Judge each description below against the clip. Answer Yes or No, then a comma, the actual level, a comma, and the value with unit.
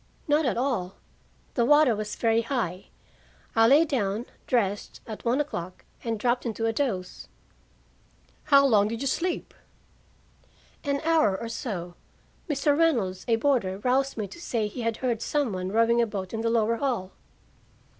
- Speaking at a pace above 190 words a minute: No, average, 165 wpm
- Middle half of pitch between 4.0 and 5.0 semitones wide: Yes, average, 4.7 semitones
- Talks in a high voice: Yes, high, 230 Hz